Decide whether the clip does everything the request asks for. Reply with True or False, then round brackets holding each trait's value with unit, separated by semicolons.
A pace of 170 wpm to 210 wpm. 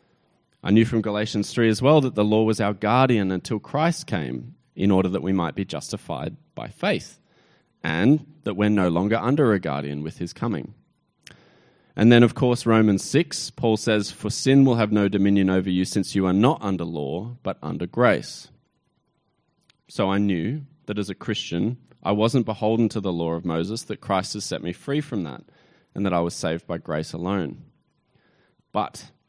True (190 wpm)